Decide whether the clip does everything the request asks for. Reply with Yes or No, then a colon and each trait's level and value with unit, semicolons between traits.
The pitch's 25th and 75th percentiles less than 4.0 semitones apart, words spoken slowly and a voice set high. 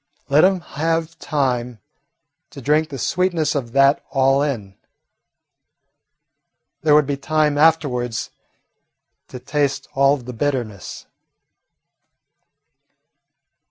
No: average, 3.1 semitones; slow, 100 wpm; medium, 140 Hz